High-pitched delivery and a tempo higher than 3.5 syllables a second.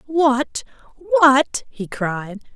No: very high, 265 Hz; 2.1 syllables/s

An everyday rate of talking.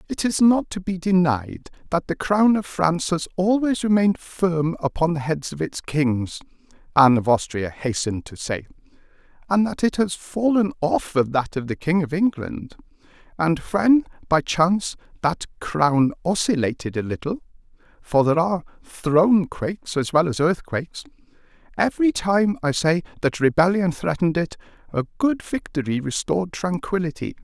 Yes: average, 150 wpm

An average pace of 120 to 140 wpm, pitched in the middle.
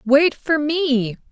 No: slow, 135 wpm; very high, 285 Hz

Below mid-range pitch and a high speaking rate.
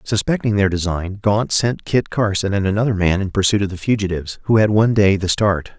Yes: low, 100 Hz; fast, 220 wpm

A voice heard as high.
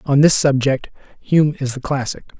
No: medium, 140 Hz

